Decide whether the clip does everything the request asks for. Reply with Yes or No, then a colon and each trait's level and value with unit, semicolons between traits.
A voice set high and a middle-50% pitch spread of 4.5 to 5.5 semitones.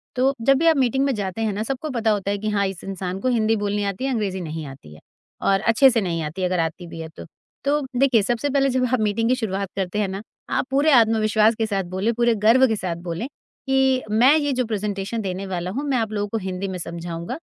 Yes: high, 215 Hz; average, 4.9 semitones